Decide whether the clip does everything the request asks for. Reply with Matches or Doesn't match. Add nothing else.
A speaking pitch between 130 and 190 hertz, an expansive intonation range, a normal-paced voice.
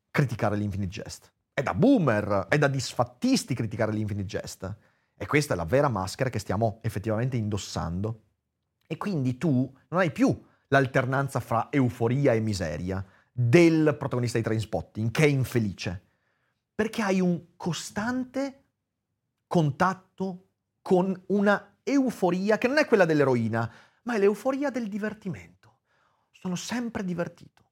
Matches